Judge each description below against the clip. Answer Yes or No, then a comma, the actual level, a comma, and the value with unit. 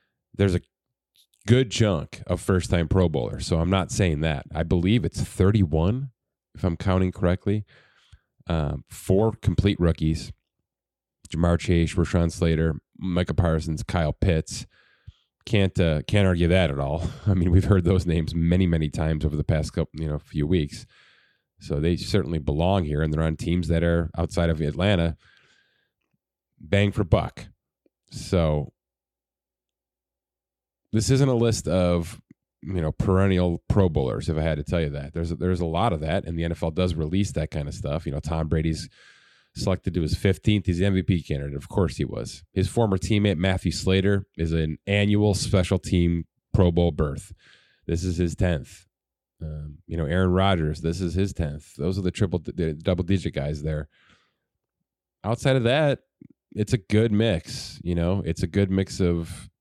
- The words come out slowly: No, average, 175 wpm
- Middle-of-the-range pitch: No, very low, 90 Hz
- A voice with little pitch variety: No, average, 3.4 semitones